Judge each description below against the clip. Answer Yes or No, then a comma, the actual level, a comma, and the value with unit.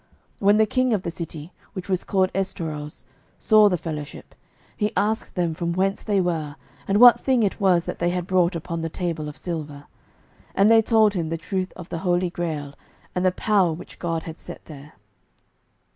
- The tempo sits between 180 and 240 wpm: Yes, average, 195 wpm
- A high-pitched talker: No, medium, 180 Hz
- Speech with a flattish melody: No, average, 3.4 semitones